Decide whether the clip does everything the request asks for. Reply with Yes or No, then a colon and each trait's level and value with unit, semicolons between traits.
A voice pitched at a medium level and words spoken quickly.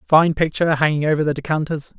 No: medium, 155 Hz; average, 180 wpm